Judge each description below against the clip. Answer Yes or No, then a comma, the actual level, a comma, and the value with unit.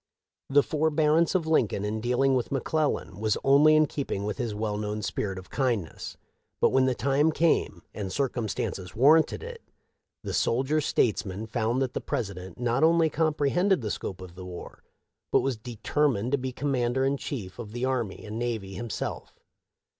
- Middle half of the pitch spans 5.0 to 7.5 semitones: Yes, average, 5.3 semitones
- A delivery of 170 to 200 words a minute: Yes, average, 175 wpm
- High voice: No, low, 125 Hz